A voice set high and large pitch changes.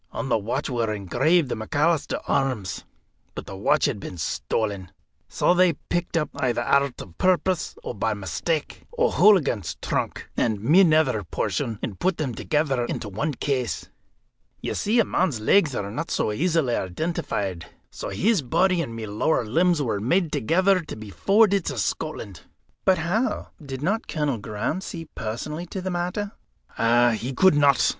No: medium, 140 Hz; wide, 7.9 semitones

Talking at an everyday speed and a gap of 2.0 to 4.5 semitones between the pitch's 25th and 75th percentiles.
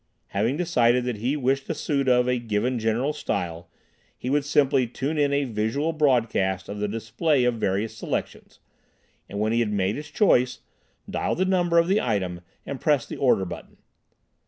No: average, 180 wpm; average, 5.0 semitones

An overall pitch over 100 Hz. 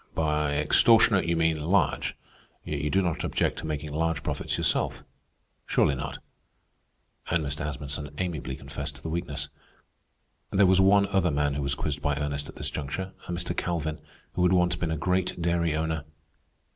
No: very low, 80 Hz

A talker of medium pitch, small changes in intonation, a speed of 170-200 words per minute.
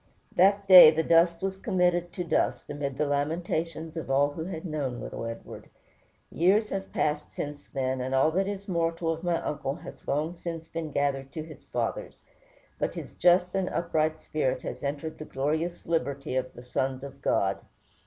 No: medium, 160 Hz; average, 3.7 semitones; average, 185 wpm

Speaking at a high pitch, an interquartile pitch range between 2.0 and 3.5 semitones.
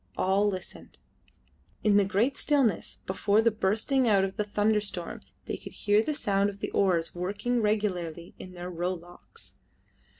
Yes: high, 200 Hz; average, 2.7 semitones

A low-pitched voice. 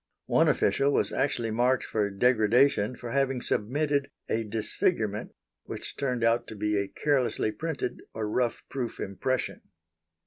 Yes: low, 120 Hz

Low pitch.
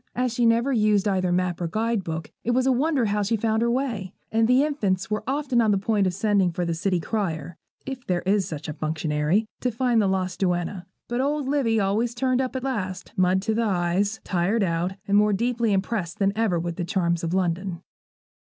No: high, 205 Hz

